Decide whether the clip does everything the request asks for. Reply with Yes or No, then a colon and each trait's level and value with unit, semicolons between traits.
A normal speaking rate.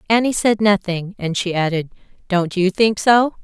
Yes: average, 175 wpm